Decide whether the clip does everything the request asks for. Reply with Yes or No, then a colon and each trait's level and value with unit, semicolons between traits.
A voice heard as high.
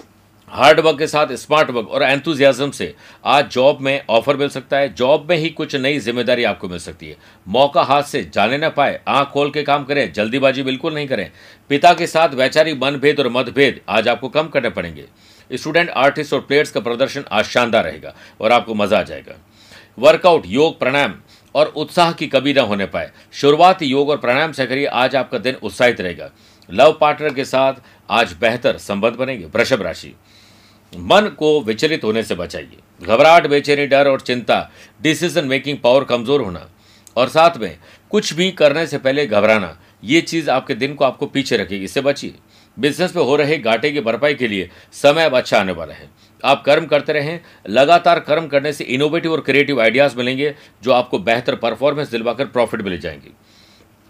No: medium, 140 Hz